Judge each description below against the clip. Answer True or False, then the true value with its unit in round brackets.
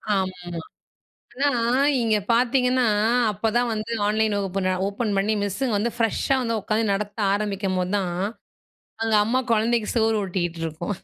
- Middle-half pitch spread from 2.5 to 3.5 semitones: True (2.9 semitones)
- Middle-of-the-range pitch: False (210 Hz)